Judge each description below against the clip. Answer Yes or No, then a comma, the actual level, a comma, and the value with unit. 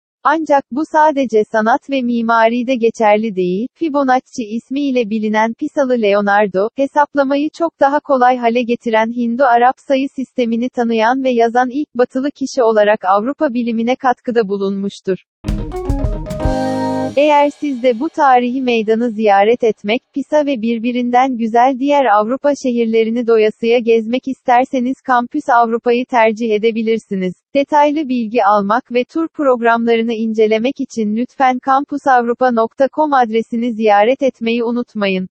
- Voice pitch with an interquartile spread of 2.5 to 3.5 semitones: Yes, average, 3.1 semitones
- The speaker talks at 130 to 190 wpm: No, average, 120 wpm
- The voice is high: Yes, high, 245 Hz